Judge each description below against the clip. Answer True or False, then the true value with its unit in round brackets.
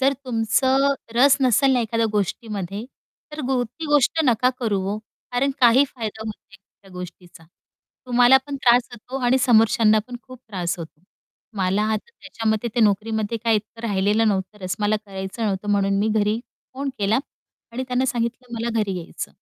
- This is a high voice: True (225 Hz)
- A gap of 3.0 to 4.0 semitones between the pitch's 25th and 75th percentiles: True (3.5 semitones)